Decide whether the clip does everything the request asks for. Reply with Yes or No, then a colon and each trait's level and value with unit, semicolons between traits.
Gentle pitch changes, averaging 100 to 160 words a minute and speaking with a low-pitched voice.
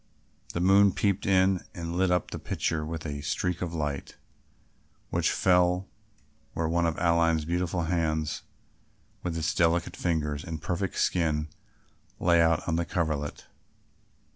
Yes: narrow, 2.1 semitones; average, 140 wpm; very low, 85 Hz